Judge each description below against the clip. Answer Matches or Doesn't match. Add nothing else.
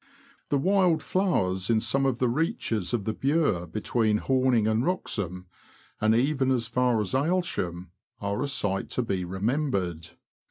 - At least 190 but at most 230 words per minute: Doesn't match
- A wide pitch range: Matches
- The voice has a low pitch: Matches